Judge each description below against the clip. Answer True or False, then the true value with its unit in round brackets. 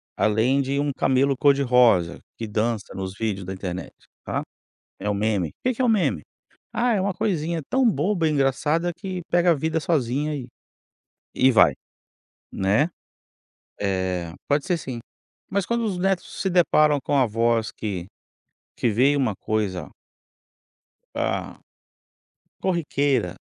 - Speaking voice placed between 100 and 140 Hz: True (135 Hz)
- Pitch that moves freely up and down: True (7.7 semitones)